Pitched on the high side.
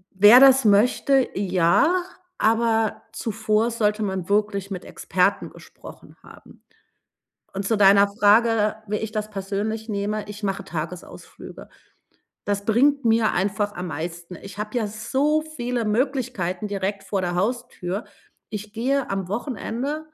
Yes: high, 210 Hz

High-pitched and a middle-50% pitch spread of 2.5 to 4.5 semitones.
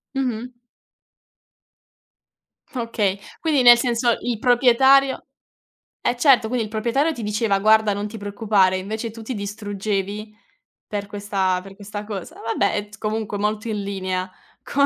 Yes: high, 215 Hz; average, 2.9 semitones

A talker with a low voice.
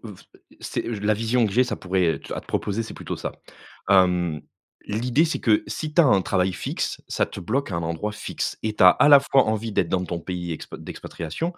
Yes: low, 105 Hz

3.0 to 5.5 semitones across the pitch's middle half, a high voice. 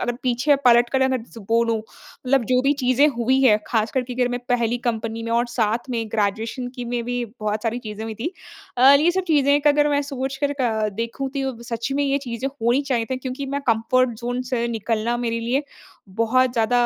No: narrow, 2.6 semitones; high, 245 Hz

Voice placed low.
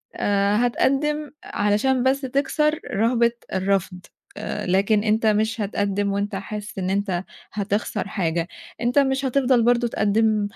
No: high, 215 Hz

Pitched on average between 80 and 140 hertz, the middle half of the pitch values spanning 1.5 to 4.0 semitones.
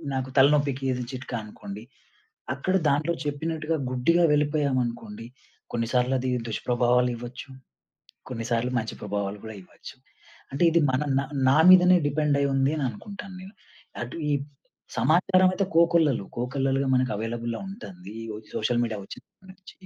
No: low, 135 Hz; average, 4.7 semitones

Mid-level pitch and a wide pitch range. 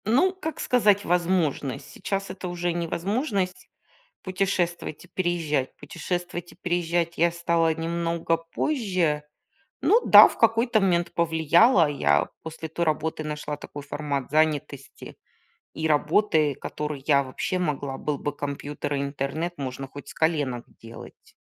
No: medium, 165 Hz; average, 3.3 semitones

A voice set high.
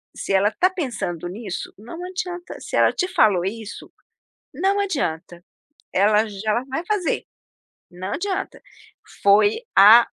Yes: high, 220 Hz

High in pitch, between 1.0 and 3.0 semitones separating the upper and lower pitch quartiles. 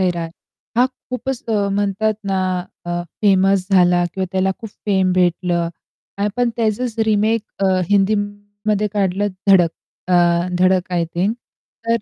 Yes: high, 200 Hz; narrow, 2.5 semitones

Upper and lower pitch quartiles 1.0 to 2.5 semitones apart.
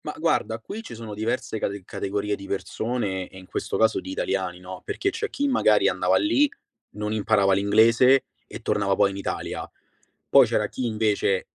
No: average, 2.9 semitones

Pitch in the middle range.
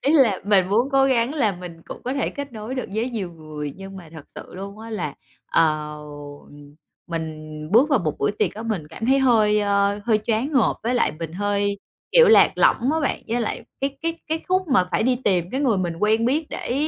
No: high, 215 Hz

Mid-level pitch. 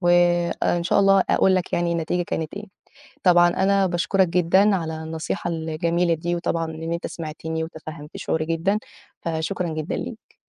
Yes: medium, 170 Hz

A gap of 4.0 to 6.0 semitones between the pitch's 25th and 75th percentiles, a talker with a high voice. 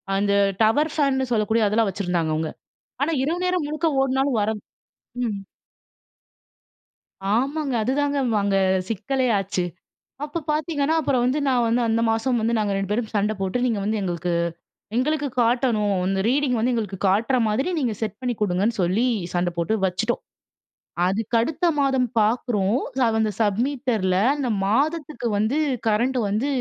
Yes: average, 4.7 semitones; high, 230 Hz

